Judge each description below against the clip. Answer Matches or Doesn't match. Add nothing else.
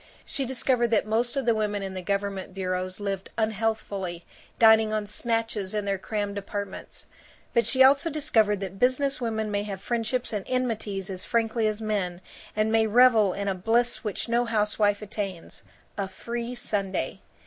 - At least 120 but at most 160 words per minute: Doesn't match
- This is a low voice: Doesn't match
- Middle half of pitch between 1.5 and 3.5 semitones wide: Matches